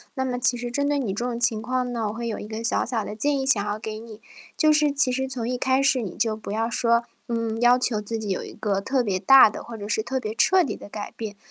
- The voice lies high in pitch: Yes, high, 235 Hz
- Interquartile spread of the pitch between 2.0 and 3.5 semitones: Yes, average, 3.0 semitones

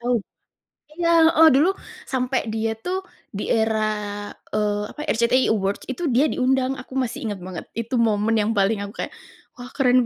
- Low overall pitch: No, high, 235 Hz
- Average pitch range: Yes, average, 3.8 semitones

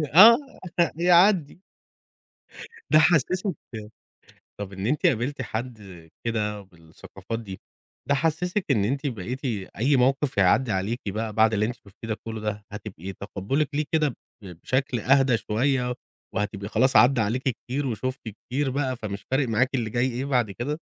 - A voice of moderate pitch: No, low, 125 Hz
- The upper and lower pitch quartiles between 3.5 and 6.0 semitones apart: Yes, average, 4.6 semitones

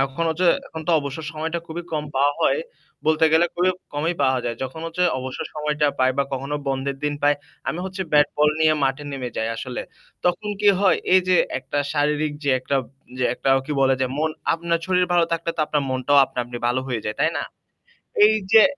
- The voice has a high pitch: No, medium, 150 Hz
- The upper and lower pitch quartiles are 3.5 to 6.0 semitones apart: Yes, average, 3.8 semitones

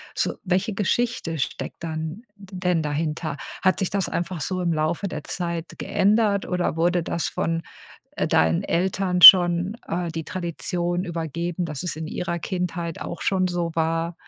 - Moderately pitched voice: Yes, medium, 175 Hz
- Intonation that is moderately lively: No, narrow, 2.2 semitones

